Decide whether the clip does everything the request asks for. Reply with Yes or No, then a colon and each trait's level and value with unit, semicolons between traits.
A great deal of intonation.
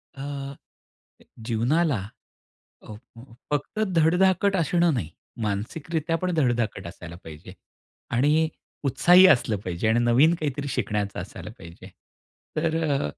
Yes: wide, 6.9 semitones